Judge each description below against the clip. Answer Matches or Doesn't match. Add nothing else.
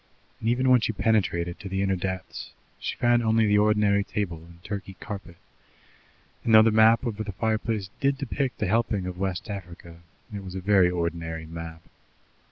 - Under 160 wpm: Doesn't match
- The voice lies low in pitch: Matches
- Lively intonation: Doesn't match